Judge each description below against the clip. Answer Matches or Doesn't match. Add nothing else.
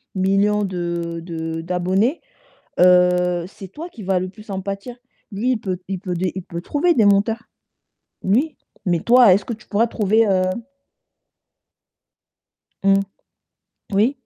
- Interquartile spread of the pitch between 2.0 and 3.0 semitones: Doesn't match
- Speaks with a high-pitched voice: Matches